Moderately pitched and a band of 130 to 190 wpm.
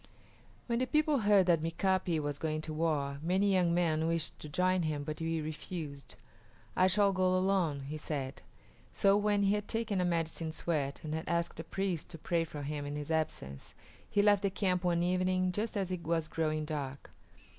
No: medium, 170 Hz; average, 200 wpm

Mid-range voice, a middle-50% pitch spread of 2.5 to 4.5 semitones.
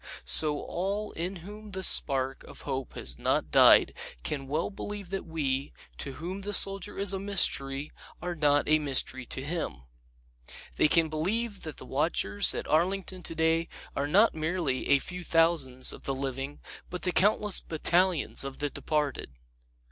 No: medium, 160 Hz; average, 5.2 semitones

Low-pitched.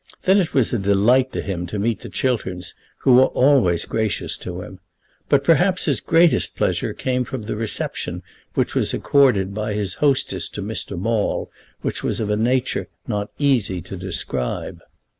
Yes: low, 110 Hz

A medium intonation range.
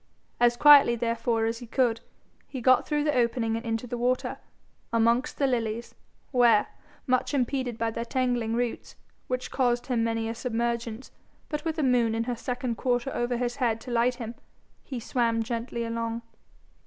No: narrow, 1.7 semitones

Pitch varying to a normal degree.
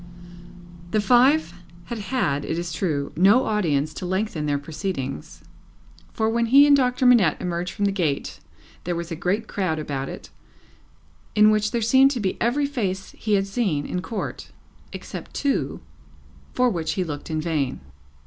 No: wide, 6.4 semitones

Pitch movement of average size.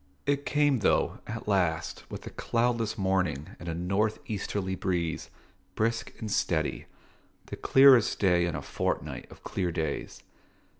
Yes: average, 4.6 semitones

